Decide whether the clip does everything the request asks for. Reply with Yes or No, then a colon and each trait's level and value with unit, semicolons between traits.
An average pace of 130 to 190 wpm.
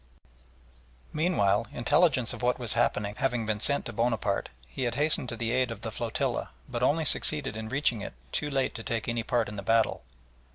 No: average, 200 wpm